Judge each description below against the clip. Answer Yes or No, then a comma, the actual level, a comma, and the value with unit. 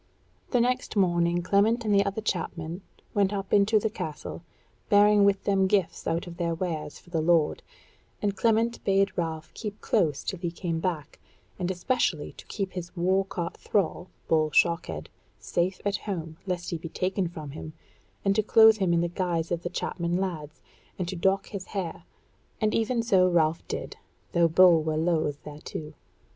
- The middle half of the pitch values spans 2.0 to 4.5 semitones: Yes, average, 3.2 semitones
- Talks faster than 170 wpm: Yes, average, 180 wpm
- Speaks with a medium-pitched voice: Yes, medium, 180 Hz